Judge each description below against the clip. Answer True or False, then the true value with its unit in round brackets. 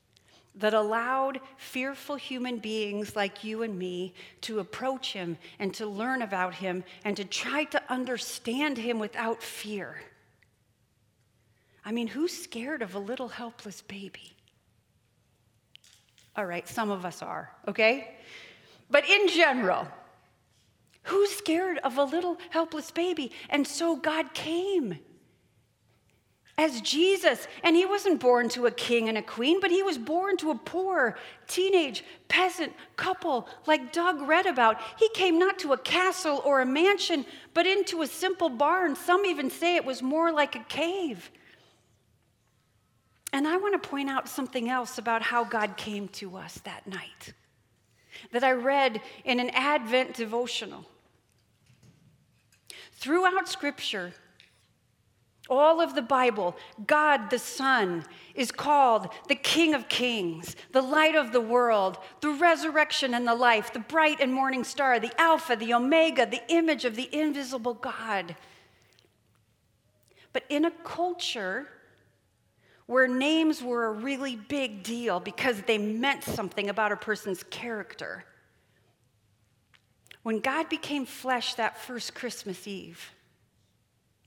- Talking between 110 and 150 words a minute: True (140 wpm)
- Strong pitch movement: True (8.4 semitones)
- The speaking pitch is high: True (245 Hz)